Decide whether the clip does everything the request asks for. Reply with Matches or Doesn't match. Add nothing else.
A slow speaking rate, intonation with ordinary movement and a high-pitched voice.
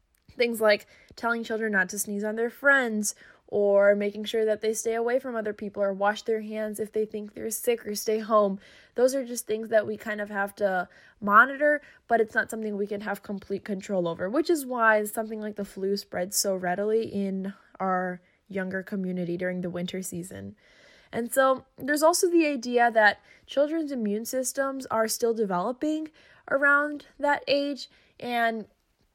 Doesn't match